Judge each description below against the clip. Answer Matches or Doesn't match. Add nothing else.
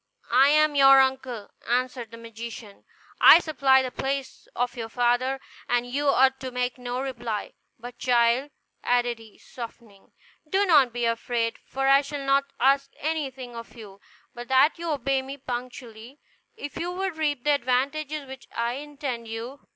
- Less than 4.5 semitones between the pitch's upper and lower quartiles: Matches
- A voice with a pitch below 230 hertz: Doesn't match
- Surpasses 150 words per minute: Matches